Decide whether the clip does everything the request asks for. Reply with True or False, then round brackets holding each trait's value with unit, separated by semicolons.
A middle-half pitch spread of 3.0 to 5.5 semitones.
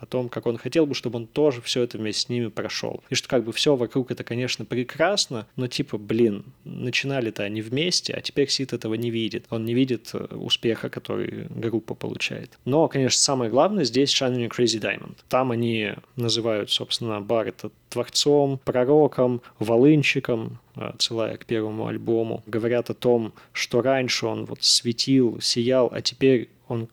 False (2.4 semitones)